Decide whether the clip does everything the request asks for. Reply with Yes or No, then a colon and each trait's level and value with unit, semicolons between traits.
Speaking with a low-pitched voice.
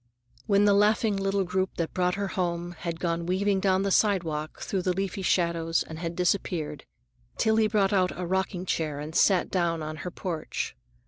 No: medium, 180 Hz